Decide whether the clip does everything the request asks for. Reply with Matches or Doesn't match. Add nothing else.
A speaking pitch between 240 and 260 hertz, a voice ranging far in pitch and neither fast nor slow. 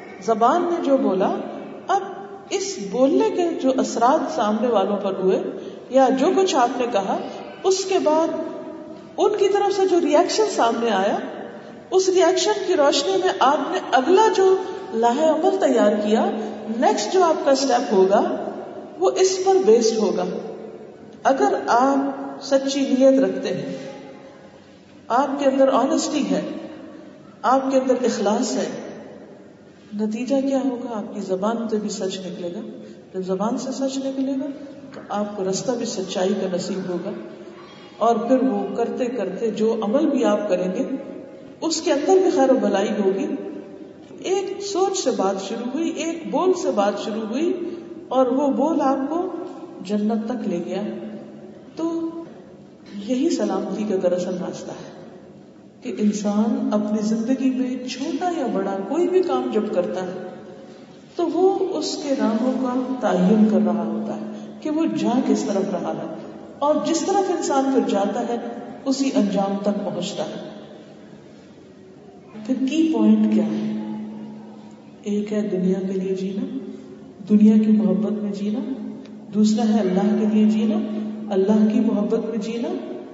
Matches